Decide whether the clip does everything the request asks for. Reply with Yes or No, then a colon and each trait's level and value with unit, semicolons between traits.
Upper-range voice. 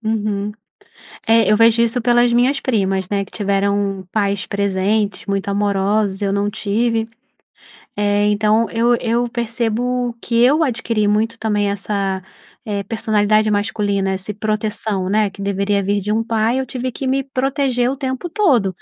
Yes: high, 215 Hz